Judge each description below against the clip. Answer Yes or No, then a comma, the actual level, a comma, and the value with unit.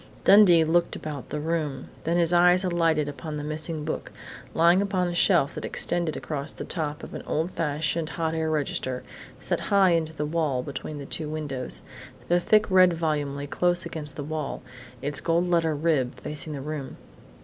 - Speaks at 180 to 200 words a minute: Yes, average, 185 wpm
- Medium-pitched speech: Yes, medium, 160 Hz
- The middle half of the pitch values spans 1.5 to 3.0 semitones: Yes, narrow, 2.6 semitones